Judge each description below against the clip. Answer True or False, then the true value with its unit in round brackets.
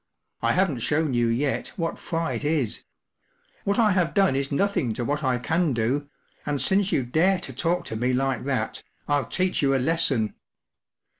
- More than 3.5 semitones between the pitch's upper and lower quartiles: True (5.1 semitones)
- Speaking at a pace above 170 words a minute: True (180 wpm)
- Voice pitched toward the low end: False (145 Hz)